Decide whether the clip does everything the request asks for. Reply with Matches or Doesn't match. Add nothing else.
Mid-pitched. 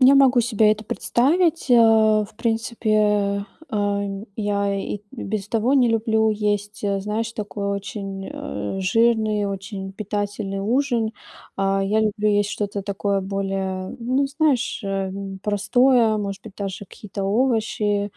Doesn't match